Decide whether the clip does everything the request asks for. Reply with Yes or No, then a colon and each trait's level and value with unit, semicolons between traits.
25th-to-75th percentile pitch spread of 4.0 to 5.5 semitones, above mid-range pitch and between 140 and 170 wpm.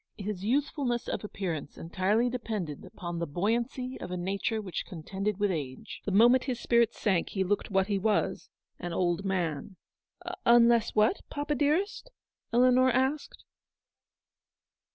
Yes: average, 4.8 semitones; high, 210 Hz; average, 155 wpm